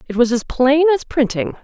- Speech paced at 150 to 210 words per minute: No, fast, 220 wpm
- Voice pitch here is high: Yes, very high, 260 Hz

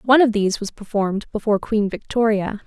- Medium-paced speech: Yes, average, 180 wpm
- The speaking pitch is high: Yes, high, 215 Hz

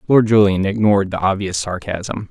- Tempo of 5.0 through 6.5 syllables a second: Yes, 5.1 syllables/s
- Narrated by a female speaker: No, male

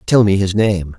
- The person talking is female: No, male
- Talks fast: Yes, fast, 245 wpm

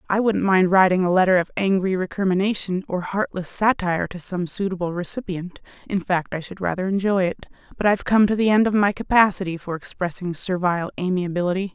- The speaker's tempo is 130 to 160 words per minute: No, average, 185 wpm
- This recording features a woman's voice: Yes, female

